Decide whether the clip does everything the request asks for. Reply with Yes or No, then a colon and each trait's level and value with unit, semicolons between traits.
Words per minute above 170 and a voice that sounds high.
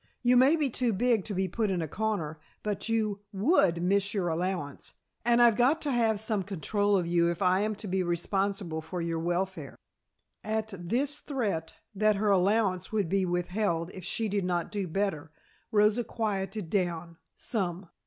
Yes: average, 180 wpm; high, 195 Hz